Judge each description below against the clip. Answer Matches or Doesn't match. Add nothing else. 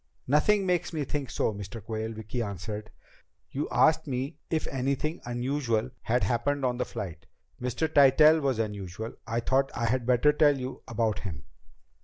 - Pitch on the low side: Matches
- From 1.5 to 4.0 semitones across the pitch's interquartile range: Doesn't match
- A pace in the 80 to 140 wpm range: Doesn't match